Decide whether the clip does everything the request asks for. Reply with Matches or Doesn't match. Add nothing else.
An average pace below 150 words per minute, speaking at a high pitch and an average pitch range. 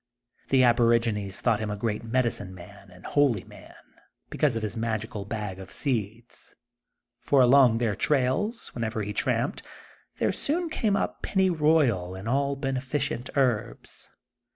Doesn't match